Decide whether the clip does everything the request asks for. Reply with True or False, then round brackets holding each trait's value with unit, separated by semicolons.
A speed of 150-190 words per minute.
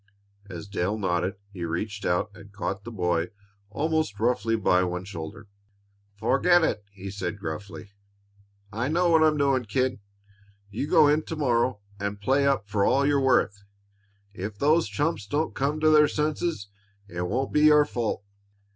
True (165 wpm)